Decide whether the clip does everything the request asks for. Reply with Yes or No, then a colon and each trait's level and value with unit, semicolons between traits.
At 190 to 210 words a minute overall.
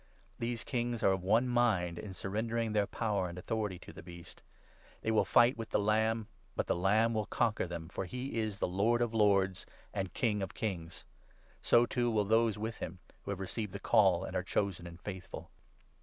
Yes: fast, 205 wpm